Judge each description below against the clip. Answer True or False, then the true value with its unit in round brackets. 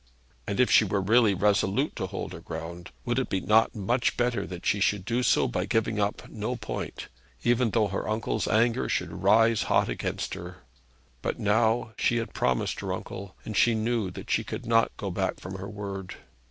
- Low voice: True (105 Hz)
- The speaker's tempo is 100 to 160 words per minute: False (200 wpm)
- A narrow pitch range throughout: False (3.1 semitones)